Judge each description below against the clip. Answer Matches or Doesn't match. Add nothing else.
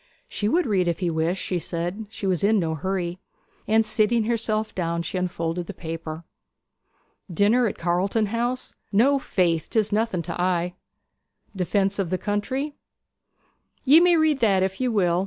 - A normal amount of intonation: Matches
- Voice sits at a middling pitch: Doesn't match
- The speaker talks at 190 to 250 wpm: Doesn't match